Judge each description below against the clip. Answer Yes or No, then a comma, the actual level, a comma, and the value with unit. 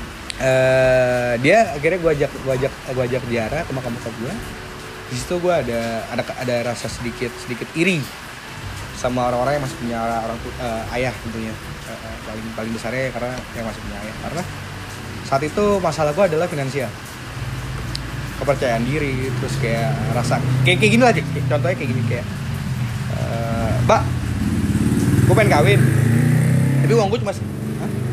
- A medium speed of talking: No, fast, 160 wpm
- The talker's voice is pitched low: Yes, low, 125 Hz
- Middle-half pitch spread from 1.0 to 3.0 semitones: Yes, narrow, 2.6 semitones